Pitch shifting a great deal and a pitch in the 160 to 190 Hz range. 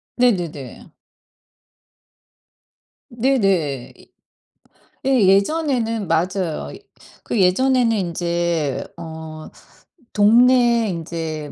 Yes: wide, 6.6 semitones; medium, 185 Hz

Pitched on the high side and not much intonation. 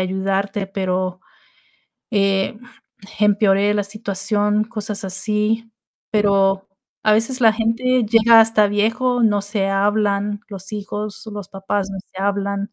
Yes: high, 205 Hz; narrow, 1.7 semitones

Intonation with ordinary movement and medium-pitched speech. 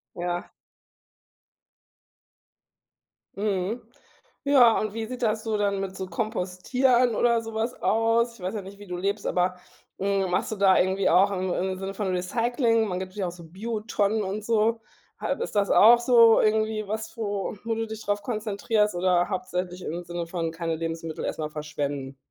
No: average, 3.5 semitones; high, 200 Hz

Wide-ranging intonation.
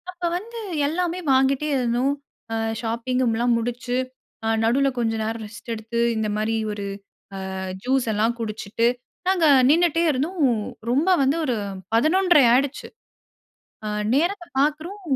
Yes: wide, 5.8 semitones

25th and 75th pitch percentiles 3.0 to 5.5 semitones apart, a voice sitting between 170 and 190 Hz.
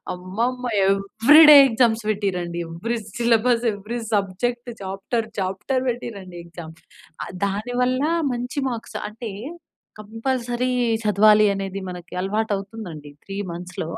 No: average, 3.8 semitones; high, 215 Hz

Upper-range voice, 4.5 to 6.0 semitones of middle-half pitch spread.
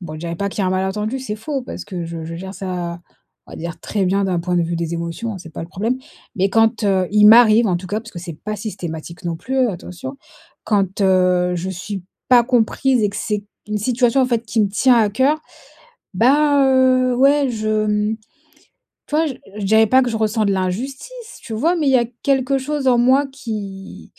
Yes: high, 215 Hz; wide, 5.5 semitones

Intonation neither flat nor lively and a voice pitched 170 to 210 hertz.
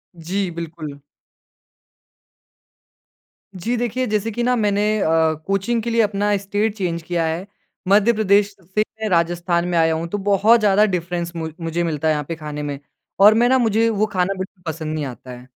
Yes: average, 4.1 semitones; high, 190 Hz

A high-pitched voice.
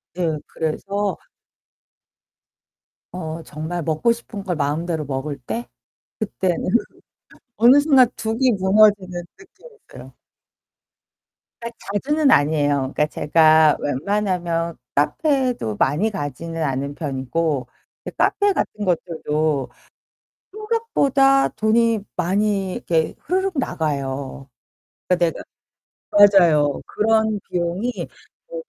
No: medium, 180 Hz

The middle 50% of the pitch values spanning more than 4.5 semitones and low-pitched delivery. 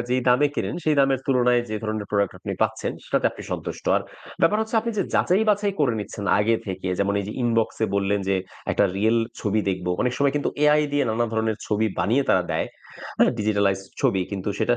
Yes: average, 5.1 semitones; low, 110 Hz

